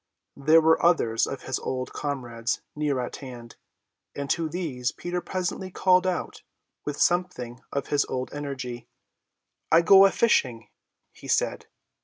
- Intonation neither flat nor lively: No, wide, 5.7 semitones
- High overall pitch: No, medium, 145 Hz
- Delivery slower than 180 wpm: Yes, average, 145 wpm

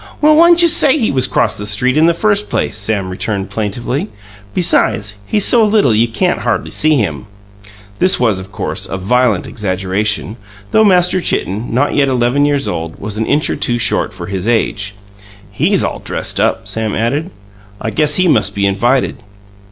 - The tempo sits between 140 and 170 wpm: No, average, 185 wpm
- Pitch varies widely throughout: Yes, wide, 7.8 semitones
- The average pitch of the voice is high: No, low, 120 Hz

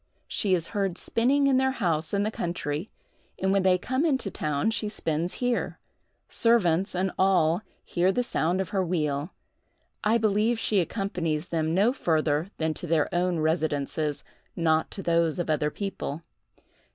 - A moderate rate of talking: Yes, average, 165 wpm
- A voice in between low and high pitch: Yes, medium, 180 Hz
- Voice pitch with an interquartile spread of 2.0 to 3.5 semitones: No, average, 4.6 semitones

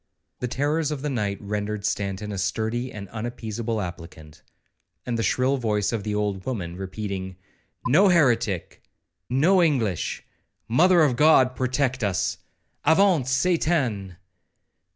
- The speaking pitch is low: Yes, low, 115 Hz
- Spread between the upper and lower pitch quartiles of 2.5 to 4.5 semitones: No, wide, 5.4 semitones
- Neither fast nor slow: No, slow, 115 wpm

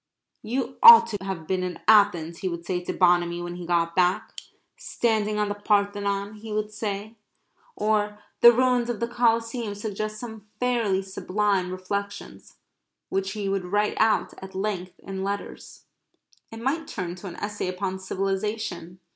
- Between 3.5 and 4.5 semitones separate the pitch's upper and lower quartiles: No, narrow, 2.6 semitones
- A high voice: Yes, high, 205 Hz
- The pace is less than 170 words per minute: Yes, average, 160 wpm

